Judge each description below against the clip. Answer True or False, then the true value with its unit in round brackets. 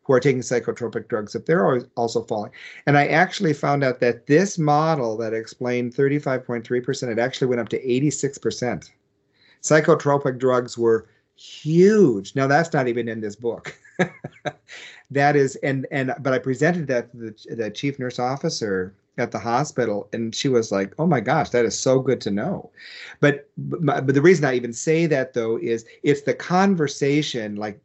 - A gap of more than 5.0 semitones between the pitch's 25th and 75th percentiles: False (3.5 semitones)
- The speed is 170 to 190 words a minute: True (175 wpm)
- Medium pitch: False (130 Hz)